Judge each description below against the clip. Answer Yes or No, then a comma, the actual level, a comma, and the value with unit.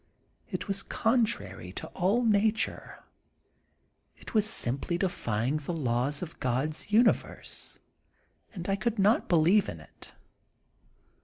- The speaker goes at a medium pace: No, slow, 120 wpm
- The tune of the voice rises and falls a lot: Yes, wide, 8.2 semitones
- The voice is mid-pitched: Yes, medium, 175 Hz